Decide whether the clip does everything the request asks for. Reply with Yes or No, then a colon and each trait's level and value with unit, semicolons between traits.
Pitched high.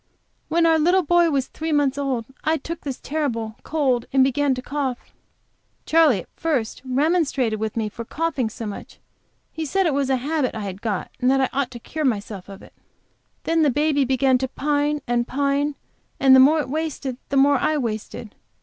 Yes: very high, 275 Hz